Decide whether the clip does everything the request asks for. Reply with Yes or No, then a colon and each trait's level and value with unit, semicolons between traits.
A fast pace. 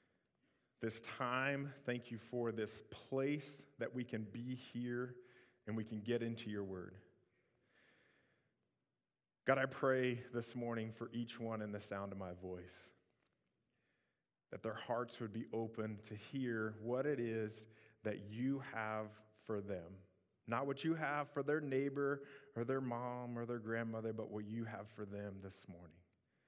No: average, 160 wpm